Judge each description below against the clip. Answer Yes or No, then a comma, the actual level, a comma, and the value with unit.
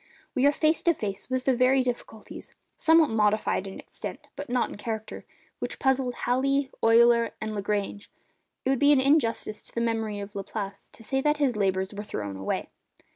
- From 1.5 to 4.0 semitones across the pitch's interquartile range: No, average, 4.4 semitones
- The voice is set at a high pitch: Yes, high, 235 Hz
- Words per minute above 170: Yes, average, 180 wpm